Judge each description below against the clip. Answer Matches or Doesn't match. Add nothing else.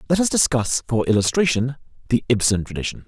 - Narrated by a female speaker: Doesn't match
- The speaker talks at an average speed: Matches